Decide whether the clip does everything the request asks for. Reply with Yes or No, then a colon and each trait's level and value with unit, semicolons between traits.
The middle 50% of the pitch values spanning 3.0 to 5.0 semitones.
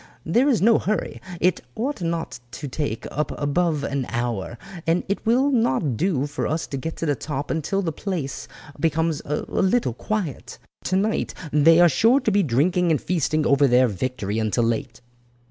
No: wide, 5.5 semitones